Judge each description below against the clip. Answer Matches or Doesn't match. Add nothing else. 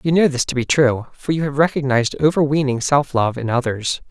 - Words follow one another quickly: Matches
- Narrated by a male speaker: Matches